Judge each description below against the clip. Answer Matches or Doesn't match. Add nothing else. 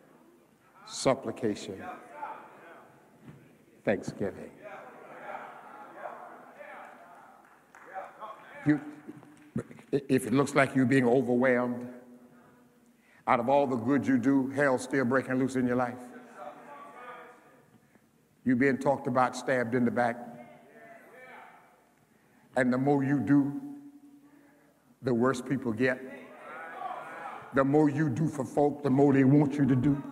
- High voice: Doesn't match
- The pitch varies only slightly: Matches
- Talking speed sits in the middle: Doesn't match